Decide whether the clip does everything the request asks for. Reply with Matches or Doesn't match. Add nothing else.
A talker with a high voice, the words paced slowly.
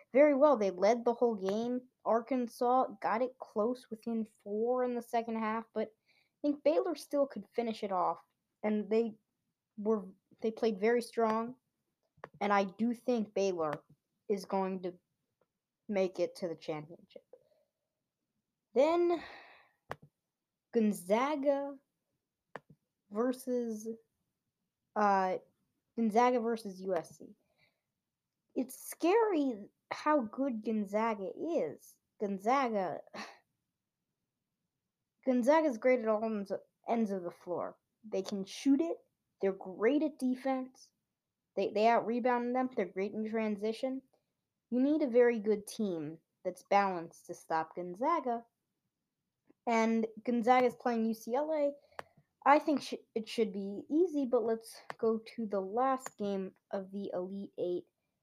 Matches